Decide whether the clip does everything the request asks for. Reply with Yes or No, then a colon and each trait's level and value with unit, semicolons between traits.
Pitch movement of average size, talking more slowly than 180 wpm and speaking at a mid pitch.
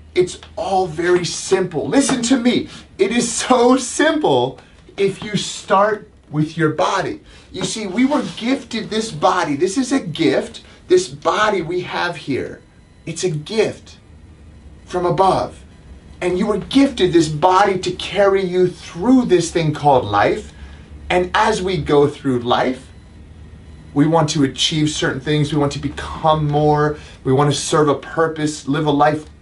No: wide, 6.0 semitones; average, 160 wpm; medium, 170 Hz